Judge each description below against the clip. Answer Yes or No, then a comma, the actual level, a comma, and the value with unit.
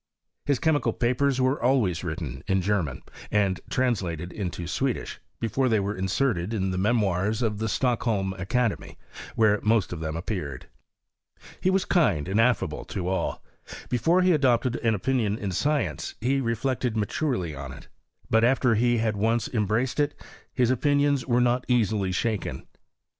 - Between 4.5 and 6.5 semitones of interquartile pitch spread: Yes, average, 4.9 semitones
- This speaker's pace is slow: No, average, 155 wpm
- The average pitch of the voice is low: Yes, low, 110 Hz